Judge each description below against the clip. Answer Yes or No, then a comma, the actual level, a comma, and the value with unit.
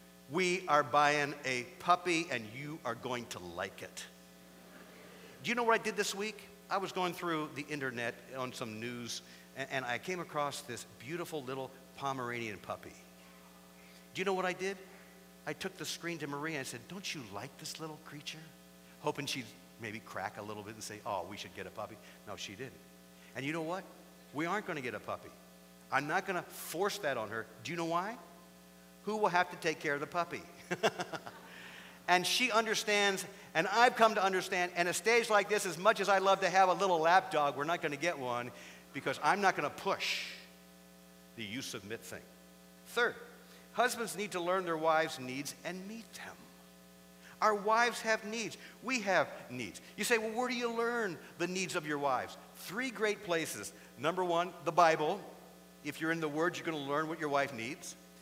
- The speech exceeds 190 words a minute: Yes, fast, 205 wpm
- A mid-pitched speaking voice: Yes, medium, 150 Hz